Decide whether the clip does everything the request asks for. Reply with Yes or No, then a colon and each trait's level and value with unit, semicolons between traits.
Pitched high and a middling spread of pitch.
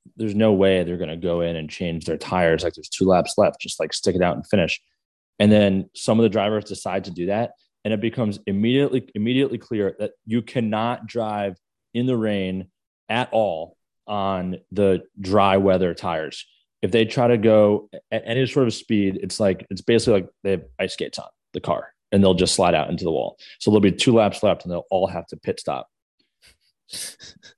No: low, 105 Hz; average, 3.2 semitones